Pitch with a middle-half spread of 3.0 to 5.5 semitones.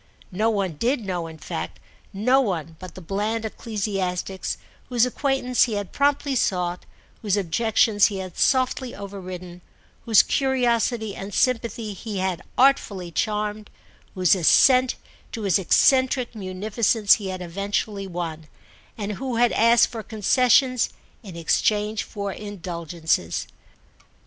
Yes: average, 4.1 semitones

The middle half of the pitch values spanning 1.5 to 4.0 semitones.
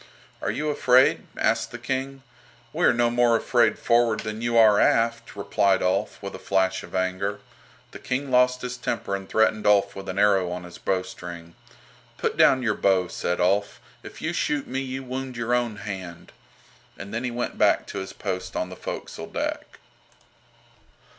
No: average, 4.5 semitones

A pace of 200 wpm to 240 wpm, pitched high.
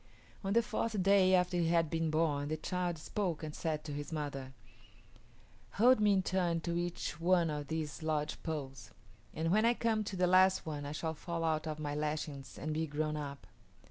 No: fast, 205 wpm; medium, 160 Hz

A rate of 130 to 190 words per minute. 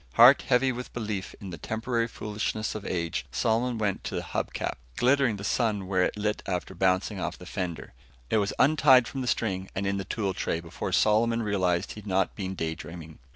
No: average, 200 wpm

